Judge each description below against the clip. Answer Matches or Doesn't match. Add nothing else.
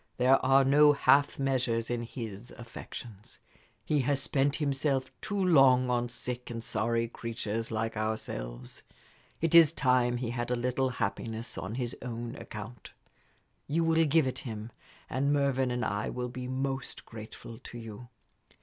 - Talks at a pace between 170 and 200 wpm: Doesn't match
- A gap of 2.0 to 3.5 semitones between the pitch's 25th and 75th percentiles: Matches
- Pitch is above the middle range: Doesn't match